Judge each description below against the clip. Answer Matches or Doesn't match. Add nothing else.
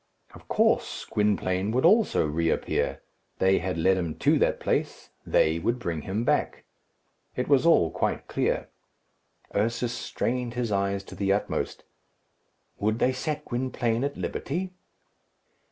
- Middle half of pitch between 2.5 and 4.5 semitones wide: Doesn't match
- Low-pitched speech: Matches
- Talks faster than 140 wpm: Doesn't match